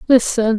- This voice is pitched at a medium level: No, high, 230 Hz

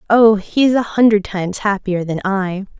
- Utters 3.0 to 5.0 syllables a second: Yes, 4.9 syllables/s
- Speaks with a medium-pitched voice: No, high, 205 Hz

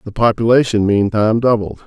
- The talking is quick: No, slow, 130 wpm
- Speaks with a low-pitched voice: Yes, low, 110 Hz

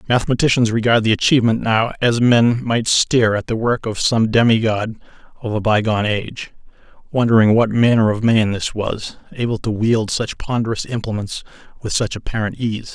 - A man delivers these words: Yes, male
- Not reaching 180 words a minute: Yes, average, 165 wpm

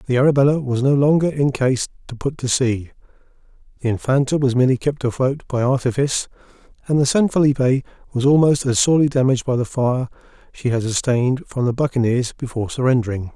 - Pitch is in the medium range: No, low, 130 Hz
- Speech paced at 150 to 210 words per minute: Yes, average, 175 wpm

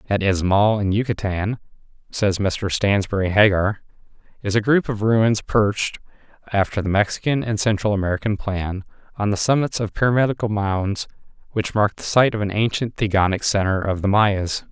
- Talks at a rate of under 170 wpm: Yes, average, 160 wpm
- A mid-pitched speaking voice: No, low, 105 Hz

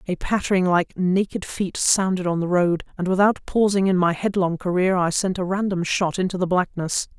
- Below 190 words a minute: No, average, 200 wpm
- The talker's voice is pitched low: No, medium, 185 Hz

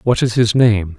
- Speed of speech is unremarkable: No, fast, 245 wpm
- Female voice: No, male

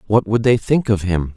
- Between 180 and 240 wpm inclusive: No, fast, 265 wpm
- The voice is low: Yes, low, 110 Hz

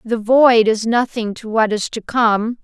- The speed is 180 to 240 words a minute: Yes, fast, 205 wpm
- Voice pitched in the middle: No, high, 225 Hz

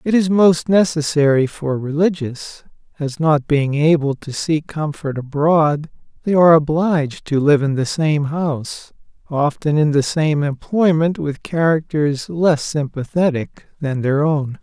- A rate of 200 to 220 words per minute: No, average, 145 wpm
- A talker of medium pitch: Yes, medium, 155 Hz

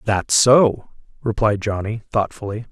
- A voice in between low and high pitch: No, low, 110 Hz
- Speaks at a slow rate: Yes, slow, 110 wpm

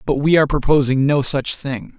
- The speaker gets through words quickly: Yes, fast, 210 wpm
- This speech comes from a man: Yes, male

